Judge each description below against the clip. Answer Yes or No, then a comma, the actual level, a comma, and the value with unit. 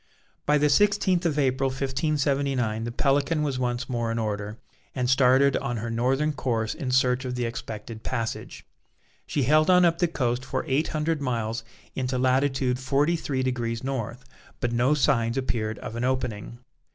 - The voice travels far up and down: No, average, 3.1 semitones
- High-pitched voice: No, low, 130 Hz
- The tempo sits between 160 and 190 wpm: Yes, average, 170 wpm